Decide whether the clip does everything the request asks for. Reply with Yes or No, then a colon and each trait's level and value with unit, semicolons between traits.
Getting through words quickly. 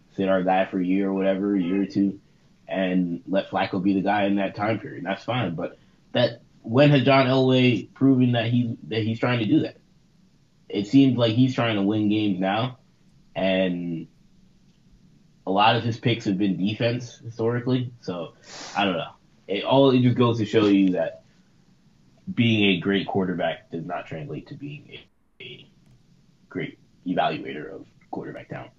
No: average, 185 wpm